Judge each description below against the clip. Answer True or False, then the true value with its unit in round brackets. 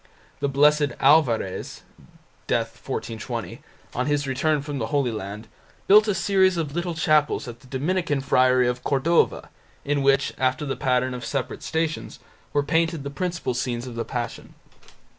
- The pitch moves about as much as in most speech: True (3.7 semitones)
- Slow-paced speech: False (160 wpm)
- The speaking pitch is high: False (135 Hz)